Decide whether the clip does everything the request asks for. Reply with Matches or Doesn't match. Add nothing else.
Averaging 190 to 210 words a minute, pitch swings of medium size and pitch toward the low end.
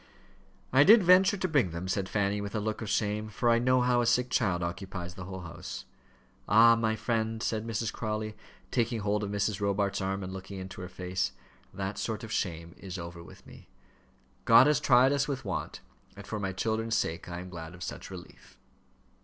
Matches